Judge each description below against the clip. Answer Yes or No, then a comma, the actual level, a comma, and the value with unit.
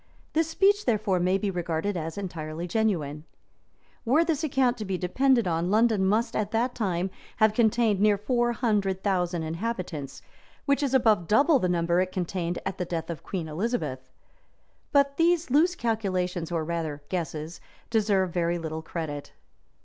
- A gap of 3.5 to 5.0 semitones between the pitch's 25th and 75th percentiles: No, wide, 5.6 semitones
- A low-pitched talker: No, high, 195 Hz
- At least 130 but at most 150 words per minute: No, average, 165 wpm